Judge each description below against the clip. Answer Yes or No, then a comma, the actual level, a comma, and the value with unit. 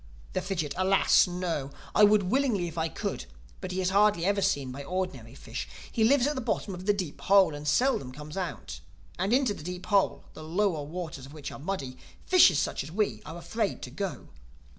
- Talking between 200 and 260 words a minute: Yes, fast, 205 wpm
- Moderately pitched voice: Yes, medium, 180 Hz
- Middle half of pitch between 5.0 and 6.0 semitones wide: Yes, average, 5.3 semitones